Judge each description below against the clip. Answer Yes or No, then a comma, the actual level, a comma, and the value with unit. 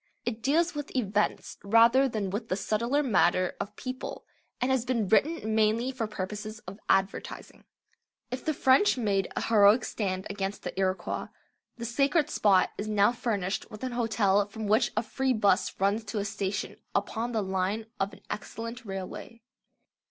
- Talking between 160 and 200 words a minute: Yes, average, 165 wpm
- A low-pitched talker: No, high, 215 Hz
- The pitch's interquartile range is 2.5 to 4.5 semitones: Yes, average, 3.4 semitones